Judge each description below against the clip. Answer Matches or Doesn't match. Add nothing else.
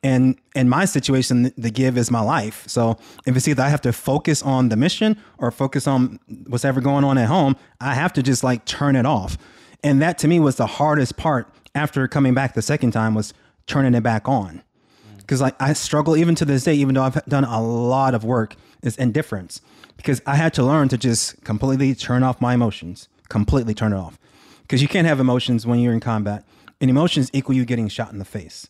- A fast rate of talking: Matches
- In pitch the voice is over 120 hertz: Matches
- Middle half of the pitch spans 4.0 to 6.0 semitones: Doesn't match